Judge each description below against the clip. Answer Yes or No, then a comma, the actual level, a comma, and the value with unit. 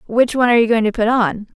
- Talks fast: Yes, fast, 305 wpm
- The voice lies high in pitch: Yes, high, 230 Hz